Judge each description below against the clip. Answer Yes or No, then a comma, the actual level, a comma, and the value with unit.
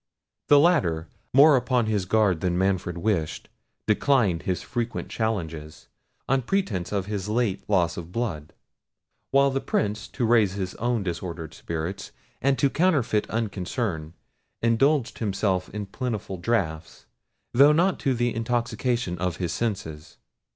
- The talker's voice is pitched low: Yes, low, 105 Hz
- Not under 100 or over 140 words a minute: Yes, slow, 135 wpm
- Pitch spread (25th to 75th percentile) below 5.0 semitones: No, wide, 5.4 semitones